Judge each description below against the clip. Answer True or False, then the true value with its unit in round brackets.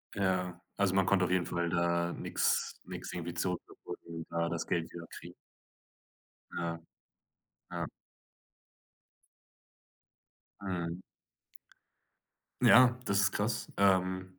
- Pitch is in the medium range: False (90 Hz)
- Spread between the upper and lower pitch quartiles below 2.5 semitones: True (2.0 semitones)